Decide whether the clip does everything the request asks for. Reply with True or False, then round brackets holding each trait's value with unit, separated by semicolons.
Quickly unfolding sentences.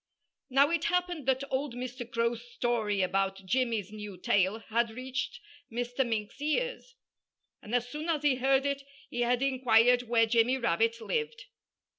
False (155 wpm)